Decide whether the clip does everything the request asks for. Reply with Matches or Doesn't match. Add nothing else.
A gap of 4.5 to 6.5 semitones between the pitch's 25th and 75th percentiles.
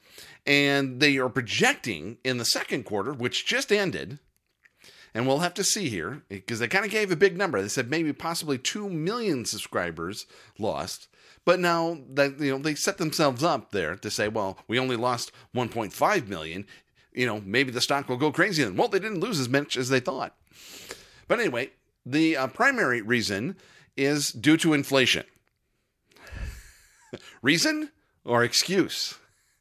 Matches